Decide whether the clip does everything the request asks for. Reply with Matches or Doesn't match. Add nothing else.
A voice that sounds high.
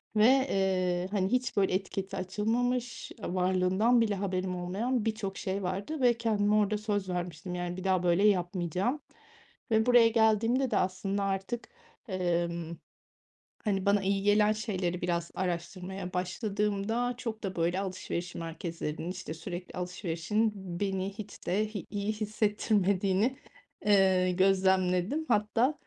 Matches